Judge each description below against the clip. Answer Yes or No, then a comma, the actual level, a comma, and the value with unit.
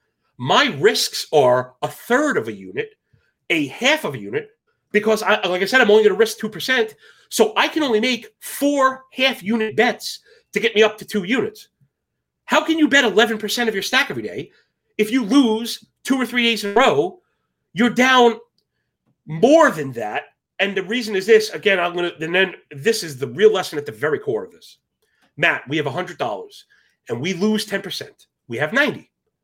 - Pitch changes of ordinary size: Yes, average, 4.5 semitones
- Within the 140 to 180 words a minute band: No, fast, 205 wpm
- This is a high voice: Yes, high, 225 Hz